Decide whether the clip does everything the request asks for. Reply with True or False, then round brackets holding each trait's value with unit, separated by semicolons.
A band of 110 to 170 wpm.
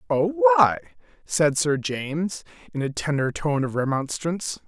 True (140 wpm)